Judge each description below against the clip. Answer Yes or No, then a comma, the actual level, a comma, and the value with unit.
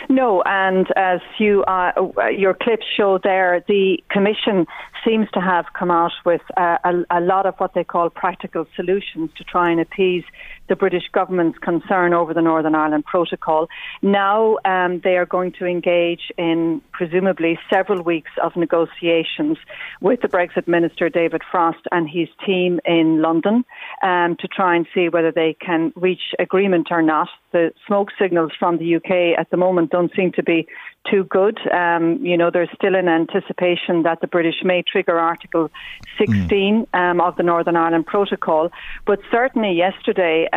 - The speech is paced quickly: No, average, 170 wpm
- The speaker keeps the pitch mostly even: Yes, narrow, 2.2 semitones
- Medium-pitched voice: Yes, medium, 180 Hz